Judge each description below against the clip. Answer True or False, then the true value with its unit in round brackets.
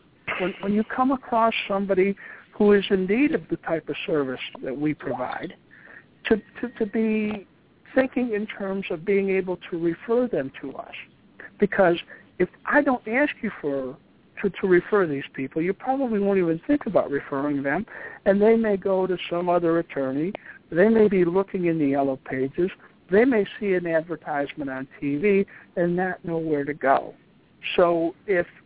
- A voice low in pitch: False (190 Hz)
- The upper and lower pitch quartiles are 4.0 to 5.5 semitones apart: True (4.4 semitones)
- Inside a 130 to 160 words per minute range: False (180 wpm)